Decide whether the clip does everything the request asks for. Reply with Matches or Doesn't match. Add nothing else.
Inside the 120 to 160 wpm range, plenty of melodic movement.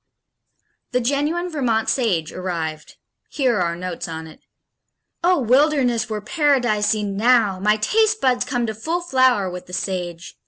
Matches